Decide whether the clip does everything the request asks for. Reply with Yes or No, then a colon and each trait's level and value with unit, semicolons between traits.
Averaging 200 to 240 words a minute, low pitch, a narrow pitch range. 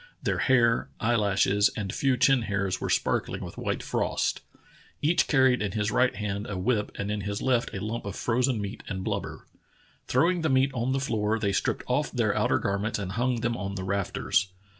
No: fast, 205 wpm; low, 110 Hz; average, 4.0 semitones